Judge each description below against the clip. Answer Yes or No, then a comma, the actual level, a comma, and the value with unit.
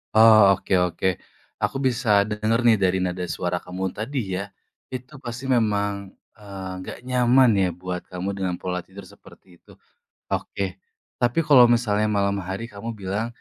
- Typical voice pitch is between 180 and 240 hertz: No, low, 100 Hz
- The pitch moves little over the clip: No, average, 4.0 semitones